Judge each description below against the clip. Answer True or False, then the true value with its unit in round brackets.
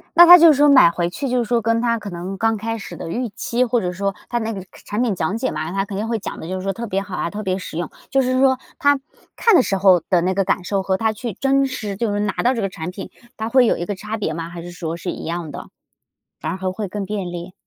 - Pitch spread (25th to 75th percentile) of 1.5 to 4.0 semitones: False (4.4 semitones)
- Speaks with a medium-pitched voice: False (200 Hz)